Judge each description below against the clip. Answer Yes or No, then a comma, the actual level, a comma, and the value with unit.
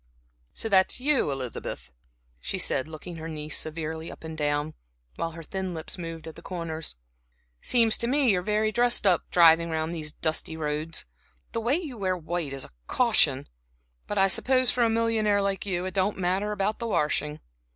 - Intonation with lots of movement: No, average, 5.0 semitones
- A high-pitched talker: No, medium, 175 Hz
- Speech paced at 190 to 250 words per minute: Yes, average, 195 wpm